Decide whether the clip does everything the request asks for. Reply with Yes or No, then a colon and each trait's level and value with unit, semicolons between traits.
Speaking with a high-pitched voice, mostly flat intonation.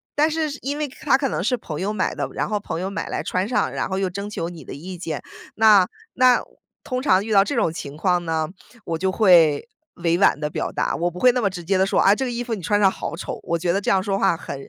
No: high, 195 Hz; average, 4.4 semitones